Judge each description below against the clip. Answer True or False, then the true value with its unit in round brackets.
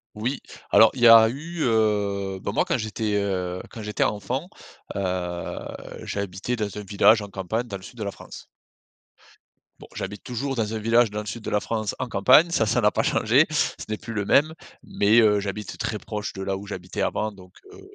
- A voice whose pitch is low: True (105 Hz)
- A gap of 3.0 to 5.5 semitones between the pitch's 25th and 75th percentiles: False (2.6 semitones)